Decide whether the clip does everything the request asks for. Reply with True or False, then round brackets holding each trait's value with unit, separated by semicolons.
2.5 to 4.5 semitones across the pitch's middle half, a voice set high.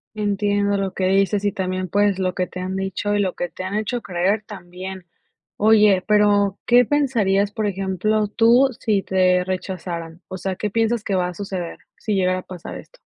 False (2.1 semitones; 195 Hz)